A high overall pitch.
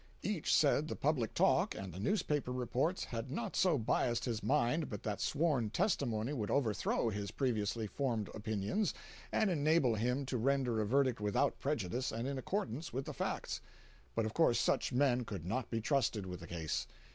No: low, 125 Hz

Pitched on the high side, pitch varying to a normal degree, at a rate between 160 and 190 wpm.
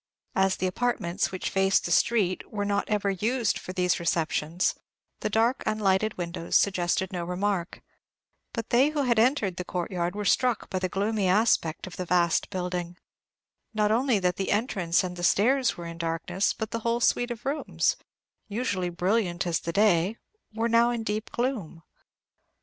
Yes: high, 195 Hz; average, 4.1 semitones; average, 170 wpm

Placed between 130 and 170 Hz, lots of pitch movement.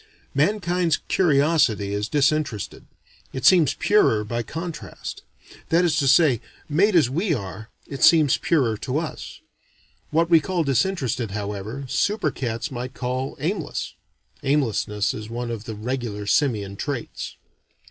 Yes: low, 135 Hz; wide, 6.3 semitones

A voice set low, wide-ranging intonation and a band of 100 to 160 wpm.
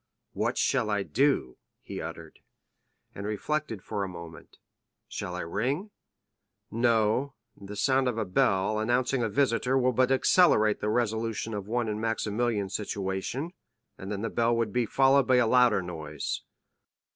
No: low, 110 Hz; average, 3.7 semitones; average, 155 wpm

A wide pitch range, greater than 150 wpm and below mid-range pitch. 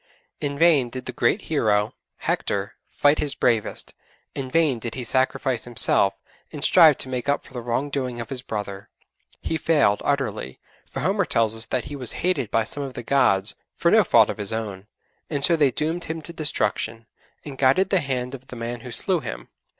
No: average, 4.2 semitones; fast, 205 wpm; low, 130 Hz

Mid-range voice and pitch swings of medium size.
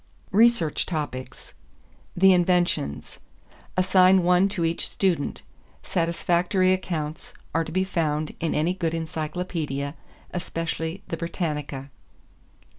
Yes: medium, 170 Hz; average, 3.1 semitones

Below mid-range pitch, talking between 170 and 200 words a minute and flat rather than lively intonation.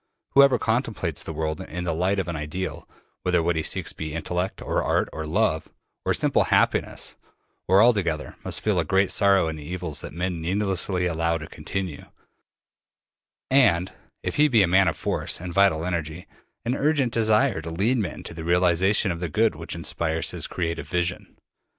No: very low, 90 Hz; average, 185 wpm; average, 3.4 semitones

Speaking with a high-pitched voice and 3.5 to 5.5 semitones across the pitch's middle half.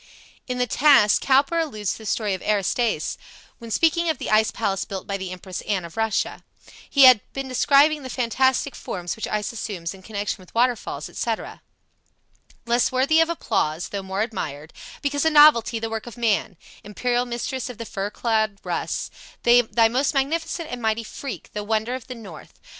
Yes: high, 230 Hz; average, 4.1 semitones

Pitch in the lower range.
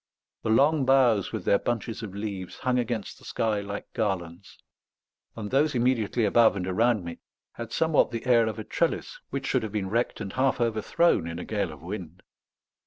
Yes: low, 110 Hz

